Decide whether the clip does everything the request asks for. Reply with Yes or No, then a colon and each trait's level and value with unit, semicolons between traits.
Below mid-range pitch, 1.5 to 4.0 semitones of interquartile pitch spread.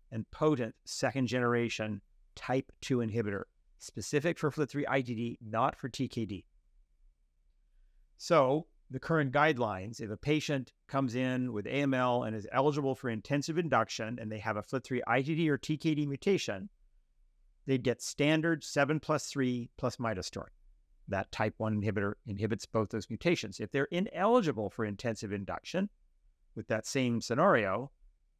No: low, 120 Hz; average, 4.7 semitones